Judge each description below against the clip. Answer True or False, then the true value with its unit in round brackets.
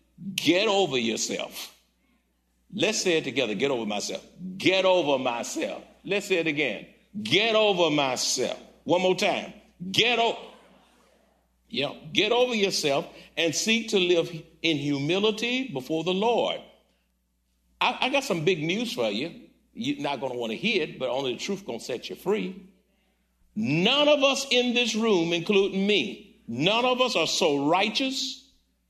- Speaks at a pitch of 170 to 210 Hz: True (190 Hz)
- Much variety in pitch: True (5.9 semitones)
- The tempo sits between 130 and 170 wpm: True (160 wpm)